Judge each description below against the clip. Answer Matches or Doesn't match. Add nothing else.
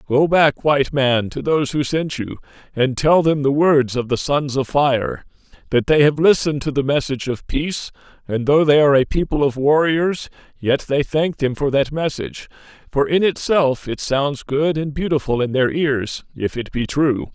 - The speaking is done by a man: Matches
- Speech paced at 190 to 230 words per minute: Matches